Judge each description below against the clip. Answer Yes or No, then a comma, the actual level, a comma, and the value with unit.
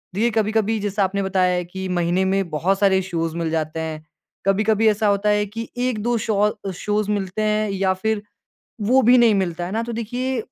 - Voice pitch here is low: No, high, 205 Hz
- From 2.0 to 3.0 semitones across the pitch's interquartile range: Yes, average, 2.7 semitones